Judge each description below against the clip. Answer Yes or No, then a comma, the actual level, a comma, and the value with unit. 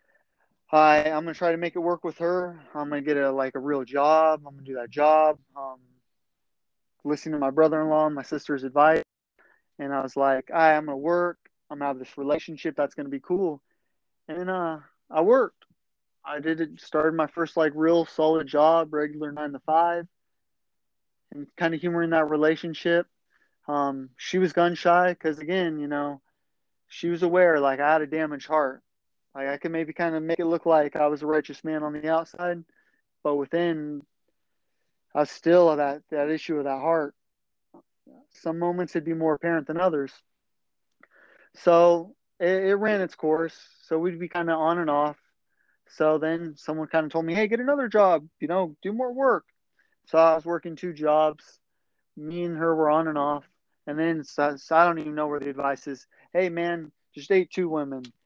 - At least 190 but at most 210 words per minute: Yes, average, 195 wpm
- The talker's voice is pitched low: No, medium, 155 Hz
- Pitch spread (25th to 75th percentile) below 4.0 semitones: Yes, narrow, 2.6 semitones